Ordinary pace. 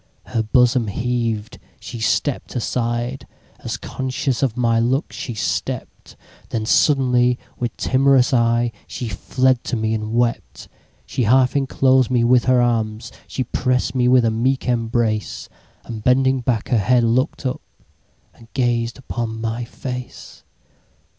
No: slow, 120 wpm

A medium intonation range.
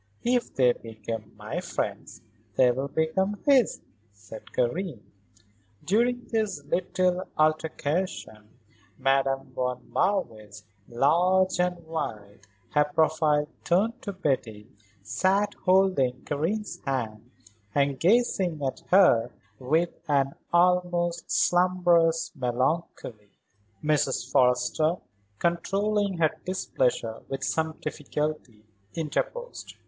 No: wide, 6.4 semitones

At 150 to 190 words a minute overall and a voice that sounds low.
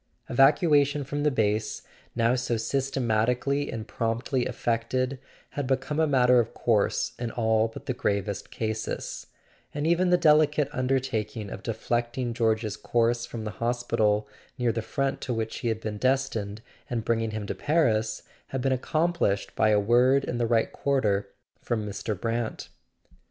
Yes: average, 160 wpm; low, 120 Hz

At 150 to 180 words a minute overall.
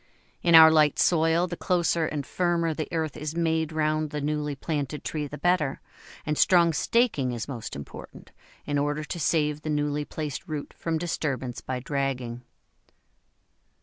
Yes: average, 160 wpm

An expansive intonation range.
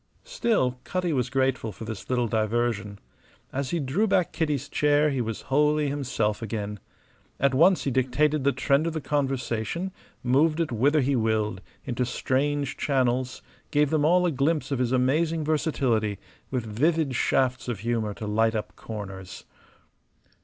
No: average, 4.6 semitones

